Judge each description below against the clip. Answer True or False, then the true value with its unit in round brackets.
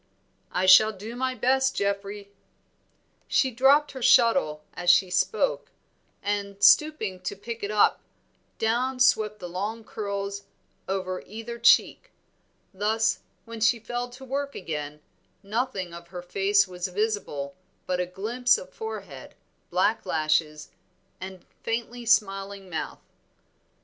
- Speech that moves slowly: True (130 wpm)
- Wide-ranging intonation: False (4.4 semitones)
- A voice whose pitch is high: True (205 Hz)